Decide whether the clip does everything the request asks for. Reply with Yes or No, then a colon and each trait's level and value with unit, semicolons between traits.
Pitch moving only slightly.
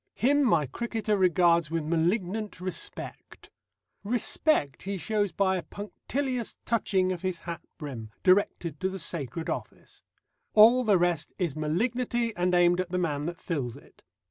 No: average, 4.2 semitones